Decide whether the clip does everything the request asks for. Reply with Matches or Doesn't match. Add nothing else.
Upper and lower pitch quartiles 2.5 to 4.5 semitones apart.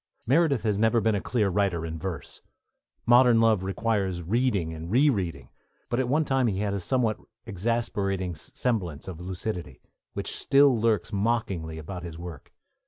Doesn't match